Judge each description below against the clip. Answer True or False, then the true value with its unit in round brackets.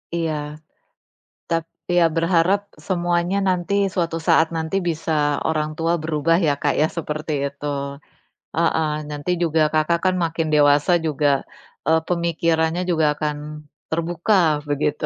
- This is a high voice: False (165 Hz)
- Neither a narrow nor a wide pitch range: False (1.8 semitones)